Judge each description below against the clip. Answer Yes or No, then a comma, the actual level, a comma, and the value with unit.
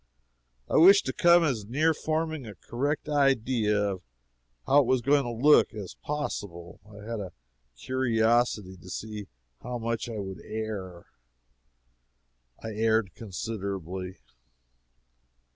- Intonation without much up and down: No, average, 5.1 semitones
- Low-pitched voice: Yes, low, 115 Hz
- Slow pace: Yes, slow, 125 wpm